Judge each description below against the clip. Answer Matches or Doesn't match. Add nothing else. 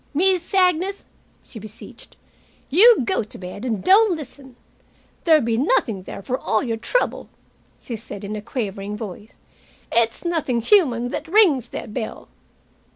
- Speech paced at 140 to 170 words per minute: Matches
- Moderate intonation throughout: Doesn't match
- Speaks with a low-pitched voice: Doesn't match